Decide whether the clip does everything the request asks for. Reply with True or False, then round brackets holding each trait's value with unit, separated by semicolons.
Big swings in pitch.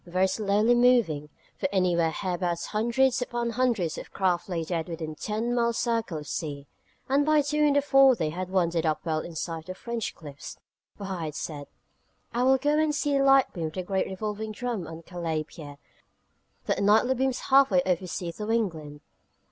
True (6.5 semitones)